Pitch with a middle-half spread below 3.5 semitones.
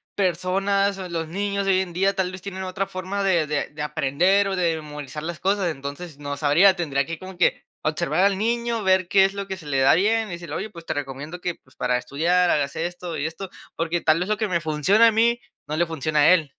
No: average, 4.2 semitones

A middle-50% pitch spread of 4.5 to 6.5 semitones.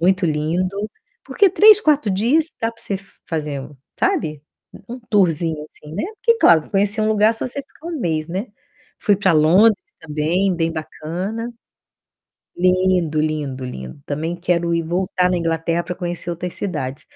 Yes: average, 4.8 semitones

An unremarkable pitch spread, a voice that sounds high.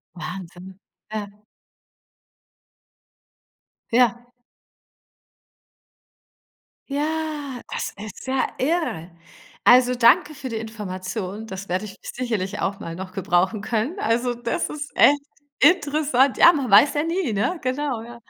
No: wide, 6.1 semitones; high, 235 Hz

